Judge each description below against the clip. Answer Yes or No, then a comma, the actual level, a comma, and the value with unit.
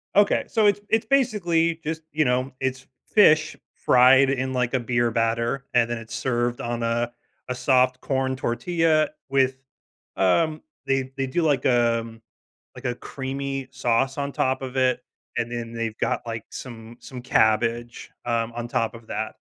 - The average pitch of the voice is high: No, low, 130 Hz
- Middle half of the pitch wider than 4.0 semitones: No, narrow, 2.6 semitones